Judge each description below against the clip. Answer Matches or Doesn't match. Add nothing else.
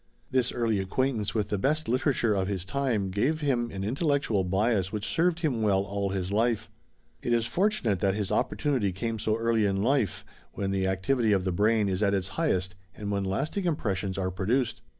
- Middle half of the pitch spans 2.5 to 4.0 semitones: Doesn't match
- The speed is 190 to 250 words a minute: Matches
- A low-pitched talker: Matches